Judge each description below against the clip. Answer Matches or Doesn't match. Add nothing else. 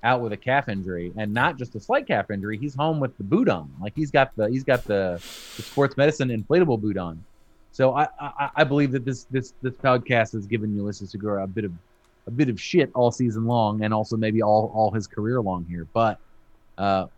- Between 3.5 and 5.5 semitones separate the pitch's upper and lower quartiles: Matches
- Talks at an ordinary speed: Doesn't match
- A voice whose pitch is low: Matches